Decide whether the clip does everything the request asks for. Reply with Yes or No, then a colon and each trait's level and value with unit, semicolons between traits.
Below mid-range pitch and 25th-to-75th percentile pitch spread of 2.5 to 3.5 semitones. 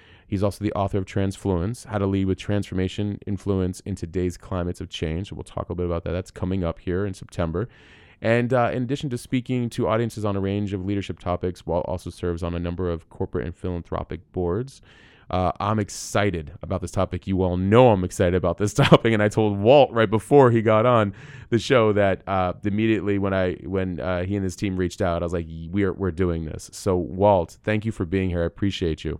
Yes: very low, 95 Hz; average, 3.0 semitones